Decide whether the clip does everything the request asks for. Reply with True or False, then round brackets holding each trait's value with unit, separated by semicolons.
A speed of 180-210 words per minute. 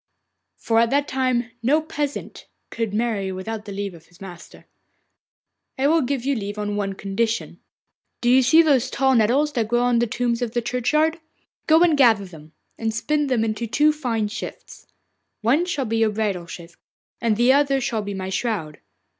True (190 wpm)